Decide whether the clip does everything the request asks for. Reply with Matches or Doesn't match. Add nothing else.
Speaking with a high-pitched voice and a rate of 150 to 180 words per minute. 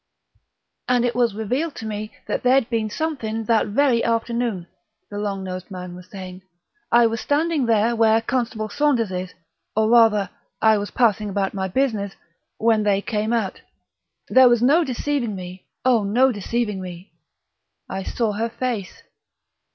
Matches